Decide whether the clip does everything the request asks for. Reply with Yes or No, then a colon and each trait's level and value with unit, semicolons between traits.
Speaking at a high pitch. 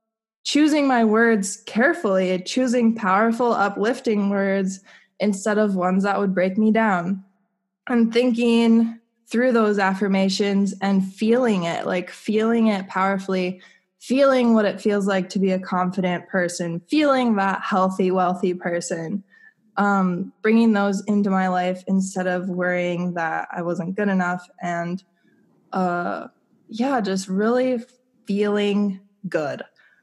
Yes: high, 200 Hz